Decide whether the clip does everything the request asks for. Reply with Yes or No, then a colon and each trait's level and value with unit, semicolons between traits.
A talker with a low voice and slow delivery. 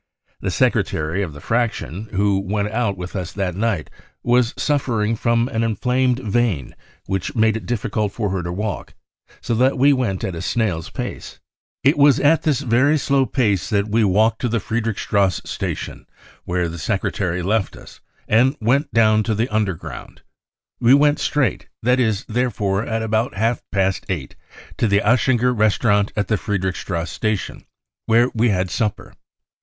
No: low, 110 Hz; average, 170 wpm